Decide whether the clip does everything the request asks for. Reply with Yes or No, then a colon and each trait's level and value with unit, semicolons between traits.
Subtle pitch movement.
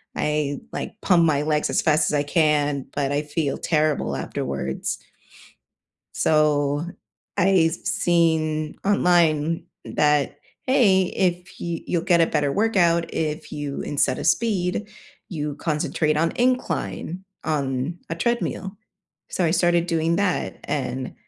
No: average, 3.0 semitones